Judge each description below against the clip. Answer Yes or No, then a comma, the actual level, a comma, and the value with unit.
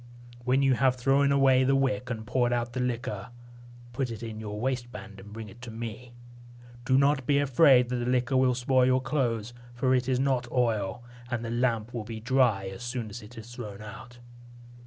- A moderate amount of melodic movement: No, narrow, 2.3 semitones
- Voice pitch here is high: No, low, 125 Hz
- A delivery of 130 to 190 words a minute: No, fast, 205 wpm